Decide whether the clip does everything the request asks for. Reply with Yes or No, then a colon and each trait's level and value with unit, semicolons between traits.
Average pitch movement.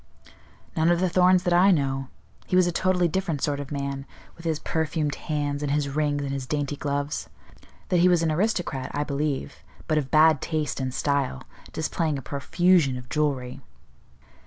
Yes: average, 3.3 semitones